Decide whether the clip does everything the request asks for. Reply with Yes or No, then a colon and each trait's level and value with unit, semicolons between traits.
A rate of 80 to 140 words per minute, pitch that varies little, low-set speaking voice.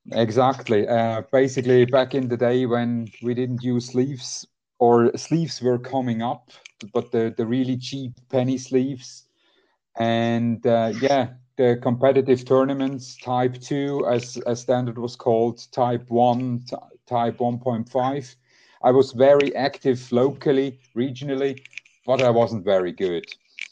Yes: slow, 135 wpm; narrow, 1.7 semitones; low, 125 Hz